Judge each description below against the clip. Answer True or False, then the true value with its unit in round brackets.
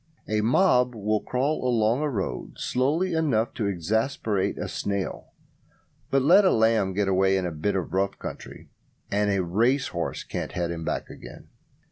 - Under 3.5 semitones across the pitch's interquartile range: False (4.9 semitones)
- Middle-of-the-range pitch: False (110 Hz)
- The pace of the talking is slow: False (165 wpm)